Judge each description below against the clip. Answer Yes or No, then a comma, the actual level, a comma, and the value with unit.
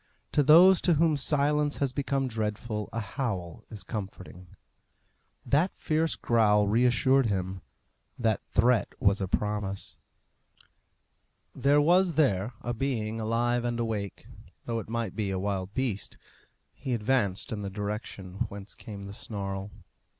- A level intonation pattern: No, average, 4.9 semitones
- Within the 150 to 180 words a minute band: No, slow, 135 wpm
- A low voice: Yes, low, 115 Hz